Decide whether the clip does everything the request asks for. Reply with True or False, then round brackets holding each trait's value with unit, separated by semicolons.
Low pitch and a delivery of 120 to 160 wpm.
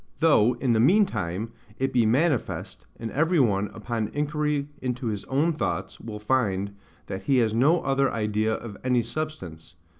False (120 Hz; 170 wpm)